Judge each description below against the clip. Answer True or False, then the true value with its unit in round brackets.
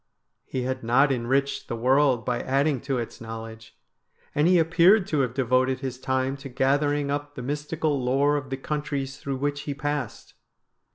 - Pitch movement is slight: True (2.3 semitones)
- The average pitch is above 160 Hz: False (135 Hz)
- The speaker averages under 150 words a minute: False (175 wpm)